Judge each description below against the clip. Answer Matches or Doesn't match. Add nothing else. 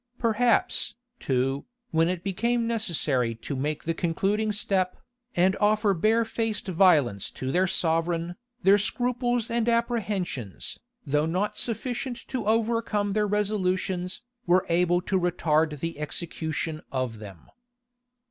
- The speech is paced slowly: Matches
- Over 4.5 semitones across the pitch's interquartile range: Matches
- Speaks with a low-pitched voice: Doesn't match